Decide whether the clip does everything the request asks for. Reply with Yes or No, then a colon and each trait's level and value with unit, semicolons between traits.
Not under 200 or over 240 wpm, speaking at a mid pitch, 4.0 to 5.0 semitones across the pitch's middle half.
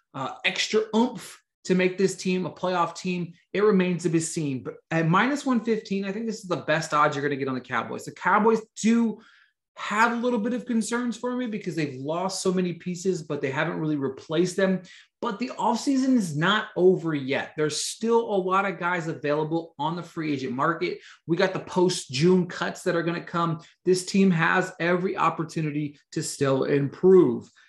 Yes: fast, 205 wpm; medium, 180 Hz; average, 4.7 semitones